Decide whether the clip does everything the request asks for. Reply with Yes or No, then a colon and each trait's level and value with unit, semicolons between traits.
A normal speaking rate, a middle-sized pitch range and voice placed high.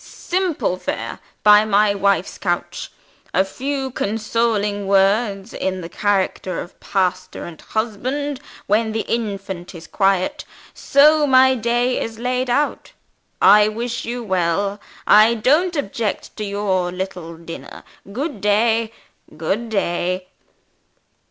No: slow, 120 wpm; average, 3.9 semitones; high, 210 Hz